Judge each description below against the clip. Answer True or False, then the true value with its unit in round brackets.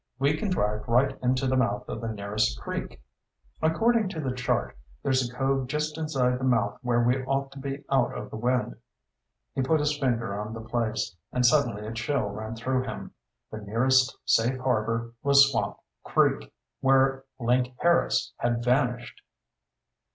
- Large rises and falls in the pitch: False (3.0 semitones)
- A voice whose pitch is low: True (125 Hz)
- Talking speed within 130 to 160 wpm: False (170 wpm)